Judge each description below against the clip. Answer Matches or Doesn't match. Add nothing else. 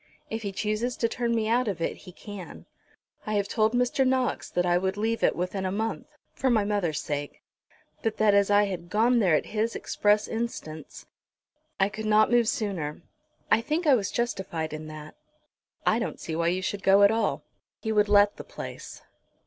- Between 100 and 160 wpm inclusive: Doesn't match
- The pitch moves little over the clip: Doesn't match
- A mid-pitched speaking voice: Doesn't match